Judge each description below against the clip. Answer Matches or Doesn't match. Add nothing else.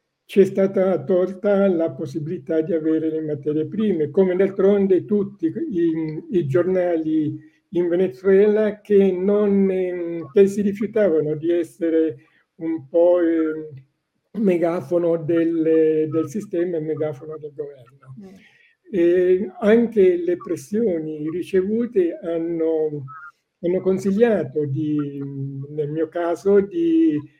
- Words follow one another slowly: Matches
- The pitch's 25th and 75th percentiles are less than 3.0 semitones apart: Doesn't match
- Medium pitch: Matches